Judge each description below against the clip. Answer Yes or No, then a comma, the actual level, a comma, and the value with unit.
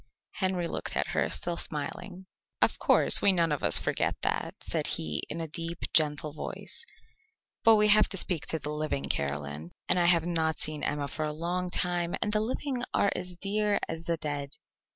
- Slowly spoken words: No, average, 195 wpm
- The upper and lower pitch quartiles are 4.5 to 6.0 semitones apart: No, average, 3.6 semitones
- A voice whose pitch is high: No, medium, 170 Hz